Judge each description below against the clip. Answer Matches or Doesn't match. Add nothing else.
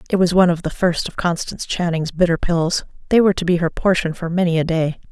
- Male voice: Doesn't match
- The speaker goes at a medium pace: Doesn't match